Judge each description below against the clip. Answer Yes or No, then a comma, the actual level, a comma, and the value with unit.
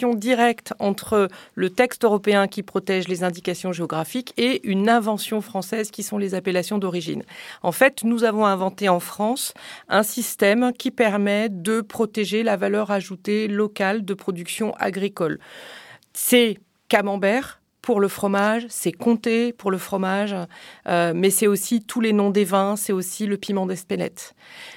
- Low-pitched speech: No, high, 205 Hz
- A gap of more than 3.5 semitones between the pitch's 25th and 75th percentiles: No, average, 2.7 semitones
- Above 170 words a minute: No, average, 155 wpm